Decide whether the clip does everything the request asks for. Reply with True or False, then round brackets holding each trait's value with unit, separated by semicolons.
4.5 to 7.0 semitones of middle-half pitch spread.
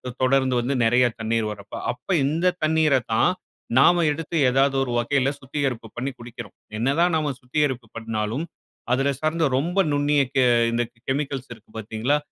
False (3.7 semitones)